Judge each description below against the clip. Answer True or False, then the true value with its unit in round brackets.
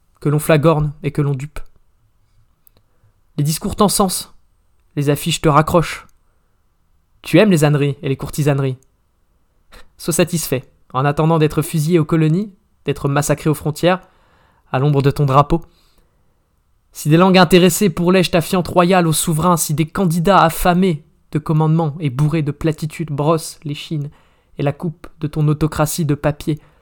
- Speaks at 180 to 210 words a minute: False (155 wpm)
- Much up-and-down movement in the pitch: False (3.3 semitones)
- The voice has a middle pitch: True (150 Hz)